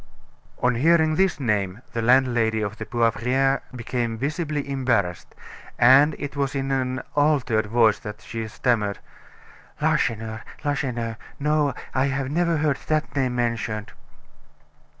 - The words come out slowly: Yes, slow, 130 wpm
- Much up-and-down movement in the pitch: No, average, 3.8 semitones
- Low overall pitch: Yes, low, 125 Hz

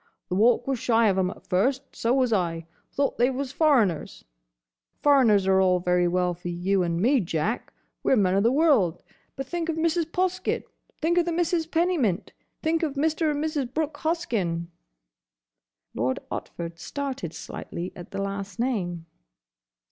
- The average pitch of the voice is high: Yes, high, 235 Hz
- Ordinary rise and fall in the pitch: No, wide, 8.8 semitones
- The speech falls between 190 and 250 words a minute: No, average, 170 wpm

